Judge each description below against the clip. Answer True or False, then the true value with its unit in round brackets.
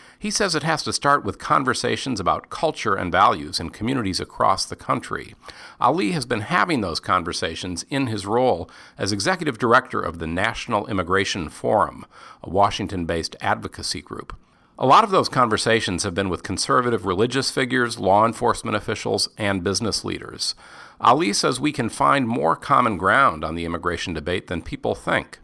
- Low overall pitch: True (100 Hz)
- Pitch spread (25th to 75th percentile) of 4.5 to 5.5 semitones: True (5.1 semitones)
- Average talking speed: True (165 wpm)